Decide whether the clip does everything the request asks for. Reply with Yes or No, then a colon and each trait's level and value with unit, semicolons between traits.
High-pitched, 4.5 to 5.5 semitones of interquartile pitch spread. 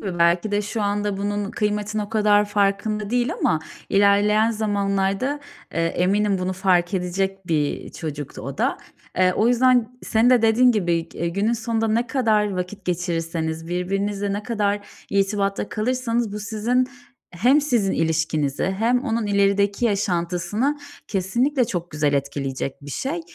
No: high, 205 Hz; average, 3.6 semitones